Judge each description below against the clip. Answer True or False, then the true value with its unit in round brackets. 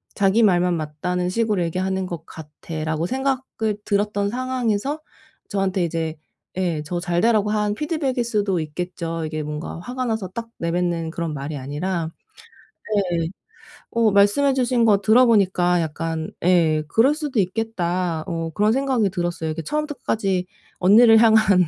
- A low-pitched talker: False (190 Hz)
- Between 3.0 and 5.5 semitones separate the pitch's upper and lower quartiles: True (5.1 semitones)